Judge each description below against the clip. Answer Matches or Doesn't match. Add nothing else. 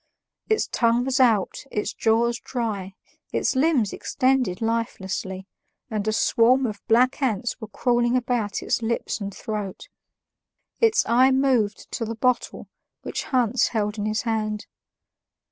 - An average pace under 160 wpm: Matches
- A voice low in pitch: Doesn't match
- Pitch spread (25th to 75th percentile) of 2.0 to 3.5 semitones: Matches